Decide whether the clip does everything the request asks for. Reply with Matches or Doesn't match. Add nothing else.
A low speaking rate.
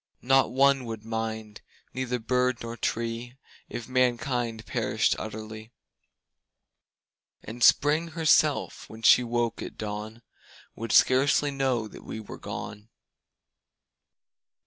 Matches